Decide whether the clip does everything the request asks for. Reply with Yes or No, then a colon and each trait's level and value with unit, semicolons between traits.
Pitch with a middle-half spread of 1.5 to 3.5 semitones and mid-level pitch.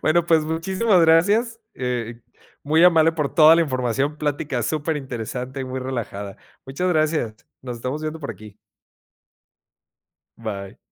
No: average, 4.7 semitones; medium, 145 Hz